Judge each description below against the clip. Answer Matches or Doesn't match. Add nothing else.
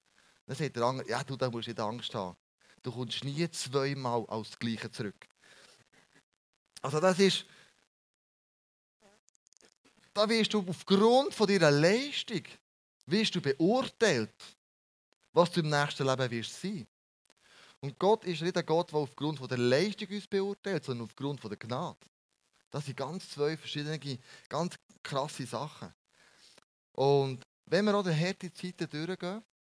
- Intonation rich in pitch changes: Matches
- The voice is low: Doesn't match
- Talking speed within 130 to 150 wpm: Matches